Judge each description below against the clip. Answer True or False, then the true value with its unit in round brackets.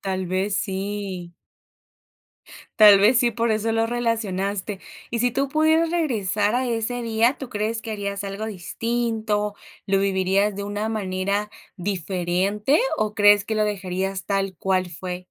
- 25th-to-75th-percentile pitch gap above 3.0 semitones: False (2.7 semitones)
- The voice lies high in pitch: True (205 Hz)